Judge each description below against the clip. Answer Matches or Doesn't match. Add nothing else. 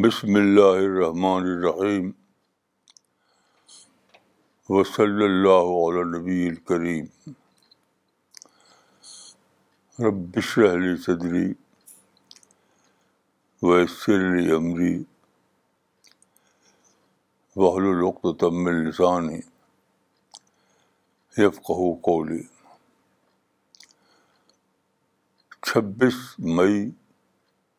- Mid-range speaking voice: Doesn't match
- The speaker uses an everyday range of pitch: Doesn't match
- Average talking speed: Doesn't match